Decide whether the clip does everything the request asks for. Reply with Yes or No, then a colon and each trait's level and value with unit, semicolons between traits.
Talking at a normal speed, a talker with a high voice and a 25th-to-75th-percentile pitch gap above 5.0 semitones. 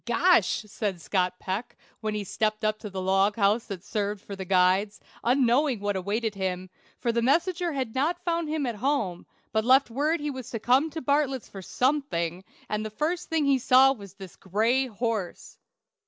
Yes: average, 190 wpm; high, 225 Hz; wide, 5.5 semitones